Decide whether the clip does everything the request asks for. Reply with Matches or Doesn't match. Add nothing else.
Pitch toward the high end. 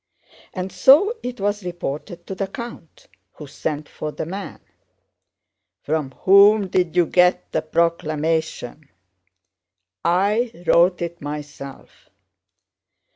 Doesn't match